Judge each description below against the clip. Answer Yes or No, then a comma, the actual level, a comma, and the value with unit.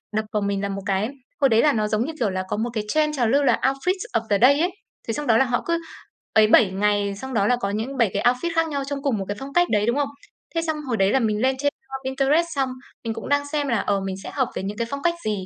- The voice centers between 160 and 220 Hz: No, high, 240 Hz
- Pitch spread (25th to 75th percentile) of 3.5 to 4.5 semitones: No, average, 5.1 semitones